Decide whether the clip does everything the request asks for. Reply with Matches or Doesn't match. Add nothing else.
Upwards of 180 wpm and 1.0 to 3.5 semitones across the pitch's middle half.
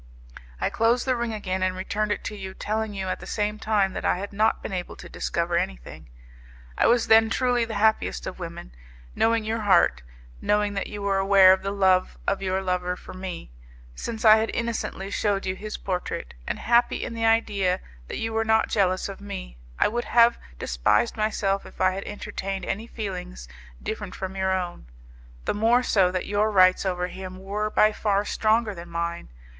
Matches